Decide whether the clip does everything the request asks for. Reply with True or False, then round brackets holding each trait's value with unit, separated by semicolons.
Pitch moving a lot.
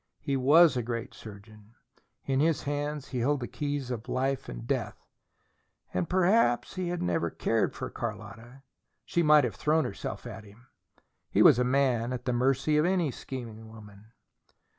False (4.7 semitones)